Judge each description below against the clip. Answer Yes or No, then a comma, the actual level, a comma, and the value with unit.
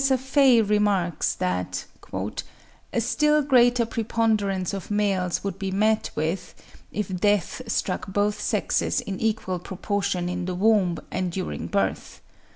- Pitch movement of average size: Yes, average, 3.4 semitones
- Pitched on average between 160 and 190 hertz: No, high, 200 Hz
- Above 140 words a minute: No, slow, 135 wpm